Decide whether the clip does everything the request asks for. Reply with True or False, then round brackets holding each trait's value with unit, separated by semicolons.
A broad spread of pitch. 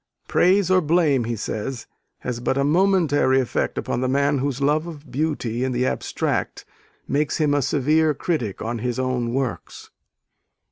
False (3.7 semitones)